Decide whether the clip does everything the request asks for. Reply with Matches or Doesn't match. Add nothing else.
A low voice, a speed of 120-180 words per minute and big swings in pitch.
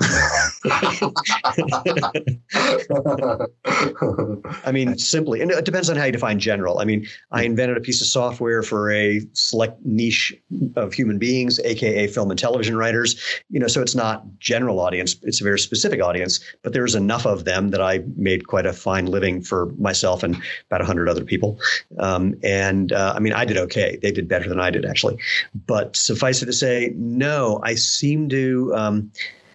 Doesn't match